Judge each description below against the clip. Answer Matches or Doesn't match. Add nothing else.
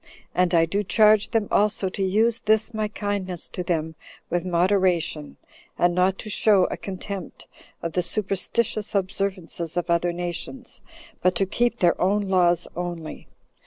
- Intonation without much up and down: Doesn't match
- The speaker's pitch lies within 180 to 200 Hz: Matches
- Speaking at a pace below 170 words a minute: Matches